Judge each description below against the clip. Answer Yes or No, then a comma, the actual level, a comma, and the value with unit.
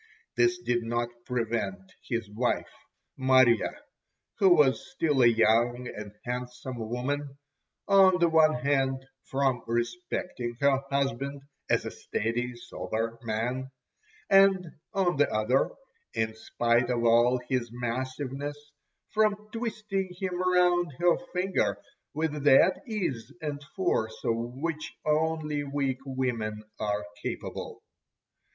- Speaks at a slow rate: Yes, slow, 120 wpm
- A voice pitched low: Yes, low, 130 Hz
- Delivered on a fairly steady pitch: No, average, 4.7 semitones